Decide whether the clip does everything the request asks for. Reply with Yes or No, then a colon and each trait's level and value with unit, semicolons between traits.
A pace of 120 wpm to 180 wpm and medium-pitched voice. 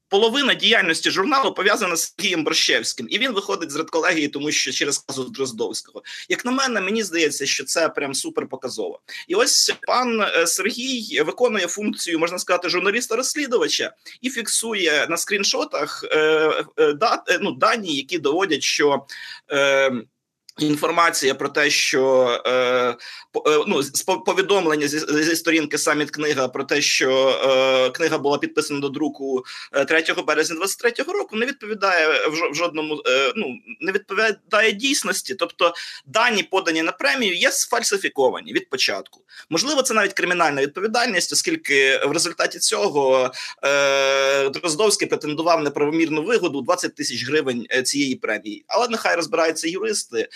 Yes: average, 140 wpm; medium, 175 Hz